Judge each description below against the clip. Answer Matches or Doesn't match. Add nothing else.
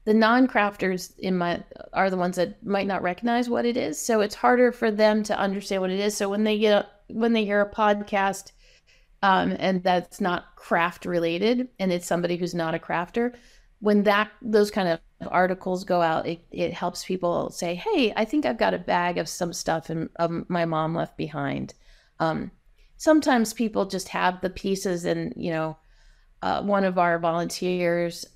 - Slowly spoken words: Doesn't match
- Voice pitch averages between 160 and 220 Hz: Matches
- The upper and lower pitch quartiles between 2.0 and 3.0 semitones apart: Doesn't match